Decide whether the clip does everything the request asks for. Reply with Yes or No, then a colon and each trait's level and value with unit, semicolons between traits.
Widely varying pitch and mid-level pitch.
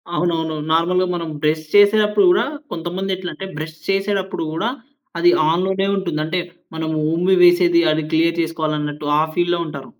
No: average, 3.0 semitones; medium, 170 Hz